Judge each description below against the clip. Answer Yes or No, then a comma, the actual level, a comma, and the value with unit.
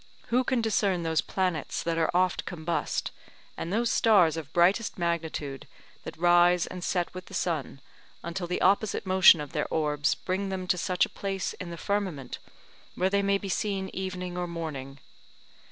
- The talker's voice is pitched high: No, medium, 180 Hz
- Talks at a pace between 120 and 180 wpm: Yes, average, 175 wpm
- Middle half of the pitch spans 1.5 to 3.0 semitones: Yes, narrow, 2.6 semitones